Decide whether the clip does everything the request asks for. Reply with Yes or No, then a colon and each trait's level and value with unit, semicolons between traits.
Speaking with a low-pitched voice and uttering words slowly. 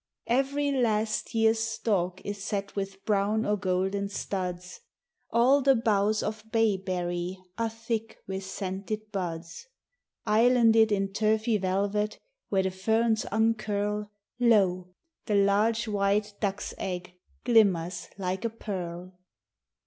No: high, 205 Hz; slow, 125 wpm